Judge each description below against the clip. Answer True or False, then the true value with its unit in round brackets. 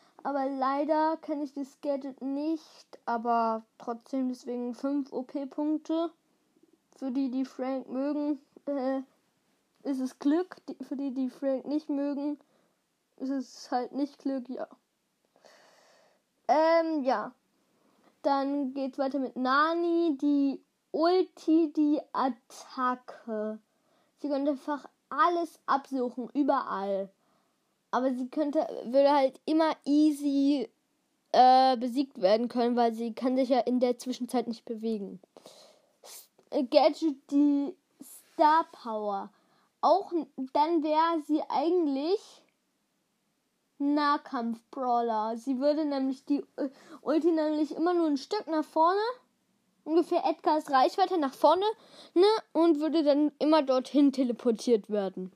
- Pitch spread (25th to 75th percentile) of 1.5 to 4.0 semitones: True (3.3 semitones)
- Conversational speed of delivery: False (115 wpm)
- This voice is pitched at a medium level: False (280 Hz)